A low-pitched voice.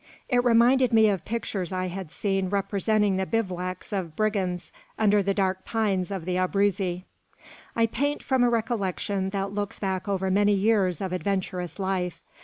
No: high, 195 Hz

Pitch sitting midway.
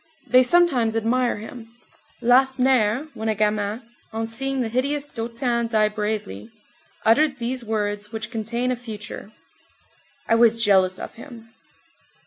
No: high, 230 Hz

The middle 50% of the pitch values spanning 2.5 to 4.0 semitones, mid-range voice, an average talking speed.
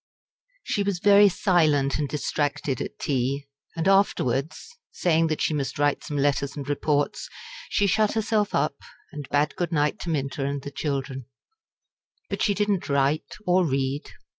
No: average, 4.5 semitones; medium, 150 Hz; average, 165 wpm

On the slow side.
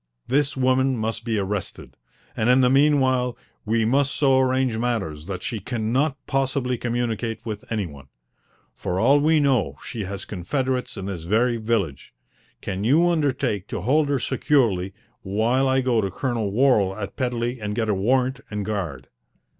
No: average, 170 wpm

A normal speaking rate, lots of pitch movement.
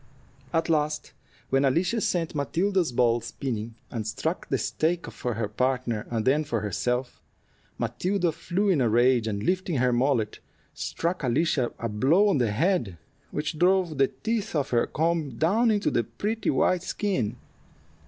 Yes: average, 160 wpm; wide, 6.6 semitones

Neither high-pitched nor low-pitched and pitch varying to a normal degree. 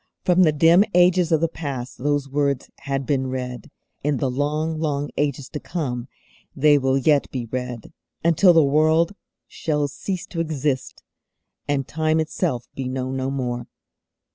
Yes: medium, 145 Hz; average, 3.3 semitones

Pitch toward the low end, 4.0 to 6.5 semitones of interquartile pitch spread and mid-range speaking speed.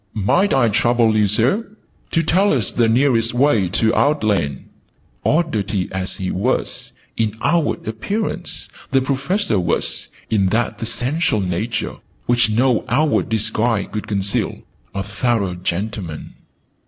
No: low, 115 Hz; average, 4.9 semitones; slow, 130 wpm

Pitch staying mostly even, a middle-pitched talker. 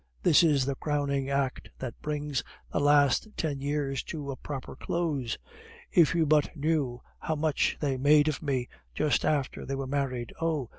Yes: narrow, 1.9 semitones; medium, 145 Hz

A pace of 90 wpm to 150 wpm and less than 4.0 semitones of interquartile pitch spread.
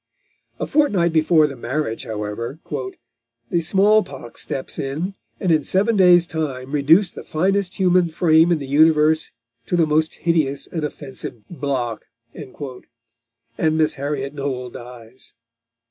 No: slow, 135 wpm; average, 4.6 semitones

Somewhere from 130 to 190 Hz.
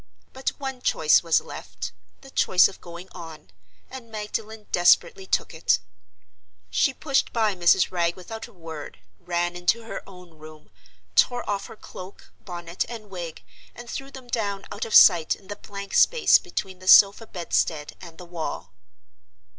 Yes: medium, 185 Hz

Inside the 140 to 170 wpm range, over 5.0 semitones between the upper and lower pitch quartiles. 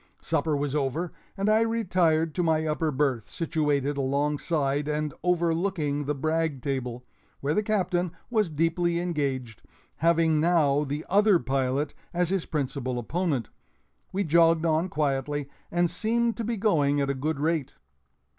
No: average, 145 wpm; average, 3.7 semitones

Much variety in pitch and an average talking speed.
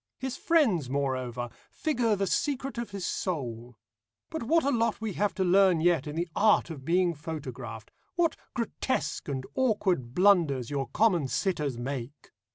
Yes: wide, 8.5 semitones; average, 160 wpm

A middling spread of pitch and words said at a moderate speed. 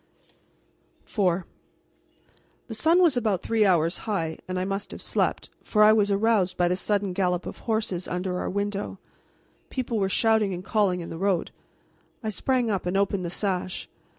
Yes: average, 3.1 semitones; average, 170 wpm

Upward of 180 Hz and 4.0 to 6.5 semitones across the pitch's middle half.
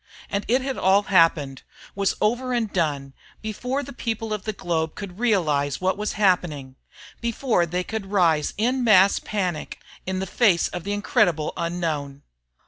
Yes: high, 190 Hz; average, 4.7 semitones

